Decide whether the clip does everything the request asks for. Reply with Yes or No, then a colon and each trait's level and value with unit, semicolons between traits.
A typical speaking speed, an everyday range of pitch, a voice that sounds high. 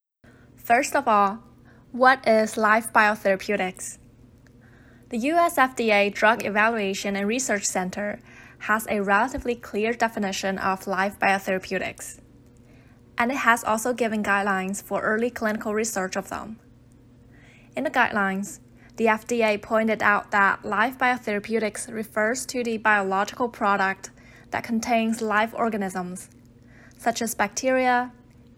No: slow, 120 wpm; average, 3.4 semitones; high, 205 Hz